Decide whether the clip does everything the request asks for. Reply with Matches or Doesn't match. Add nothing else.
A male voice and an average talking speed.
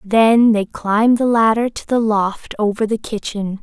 Doesn't match